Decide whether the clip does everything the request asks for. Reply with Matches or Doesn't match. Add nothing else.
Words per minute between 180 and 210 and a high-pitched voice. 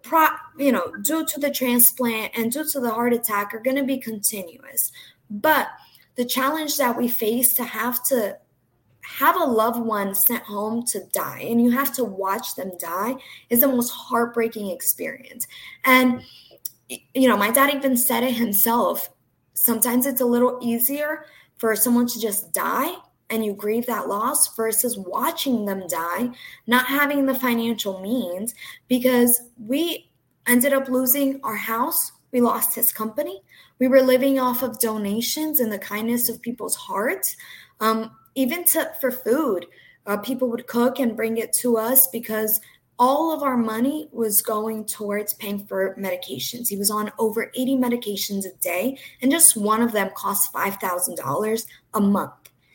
Doesn't match